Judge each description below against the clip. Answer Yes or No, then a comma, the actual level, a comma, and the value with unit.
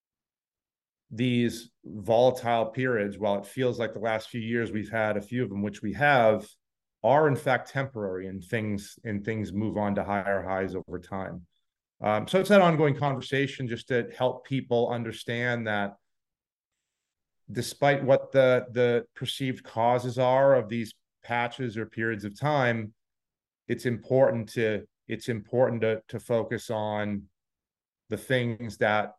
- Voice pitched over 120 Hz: No, low, 115 Hz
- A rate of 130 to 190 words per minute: Yes, average, 150 wpm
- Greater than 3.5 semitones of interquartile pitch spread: No, average, 3.2 semitones